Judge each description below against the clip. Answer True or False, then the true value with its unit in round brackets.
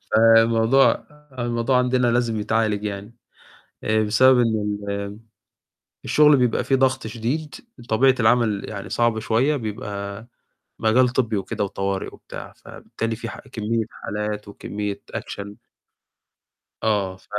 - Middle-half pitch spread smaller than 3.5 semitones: True (2.8 semitones)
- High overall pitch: False (110 Hz)